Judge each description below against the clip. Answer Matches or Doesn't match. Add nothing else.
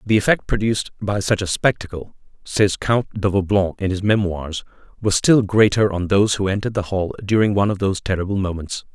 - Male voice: Matches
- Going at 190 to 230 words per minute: Matches